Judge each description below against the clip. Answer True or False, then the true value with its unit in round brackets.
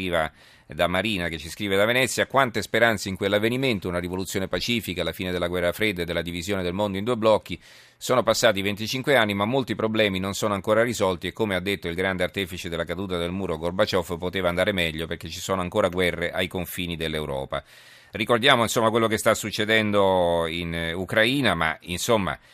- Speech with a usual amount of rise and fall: True (3.8 semitones)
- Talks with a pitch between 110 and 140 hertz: False (95 Hz)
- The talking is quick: True (190 wpm)